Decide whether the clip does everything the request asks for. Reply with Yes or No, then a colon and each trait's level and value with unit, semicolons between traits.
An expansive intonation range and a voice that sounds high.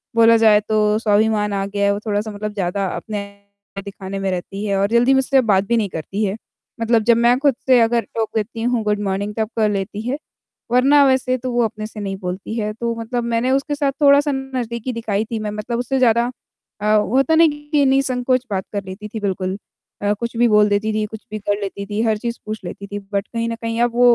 No: average, 3.0 semitones; high, 220 Hz